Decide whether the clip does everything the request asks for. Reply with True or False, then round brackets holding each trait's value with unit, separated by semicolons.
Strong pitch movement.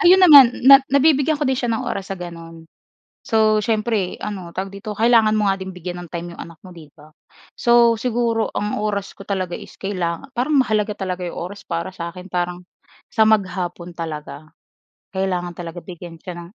False (4.3 semitones)